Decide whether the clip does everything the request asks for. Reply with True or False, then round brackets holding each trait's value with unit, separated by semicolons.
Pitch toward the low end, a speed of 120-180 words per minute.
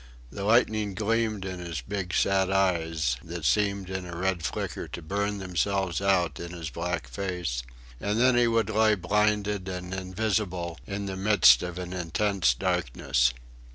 True (95 Hz; 160 wpm)